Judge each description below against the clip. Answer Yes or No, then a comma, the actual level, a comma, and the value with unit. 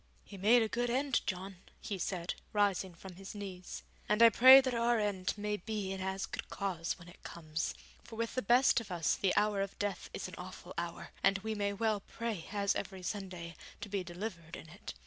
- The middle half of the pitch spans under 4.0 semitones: Yes, average, 3.1 semitones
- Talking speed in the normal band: No, fast, 215 wpm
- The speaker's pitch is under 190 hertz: No, high, 200 Hz